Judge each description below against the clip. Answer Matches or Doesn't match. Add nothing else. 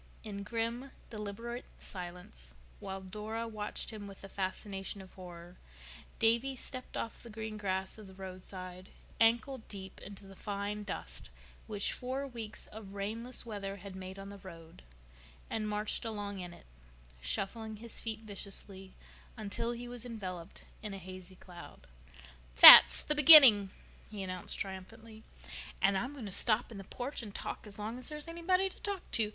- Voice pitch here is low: Doesn't match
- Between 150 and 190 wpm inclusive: Matches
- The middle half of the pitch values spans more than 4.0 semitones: Doesn't match